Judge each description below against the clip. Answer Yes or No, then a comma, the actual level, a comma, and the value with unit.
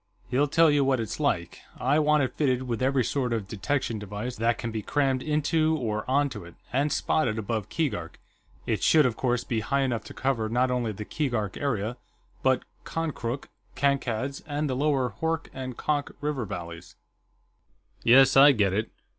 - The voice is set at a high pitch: No, low, 130 Hz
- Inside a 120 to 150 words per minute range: No, average, 180 wpm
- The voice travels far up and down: No, average, 4.2 semitones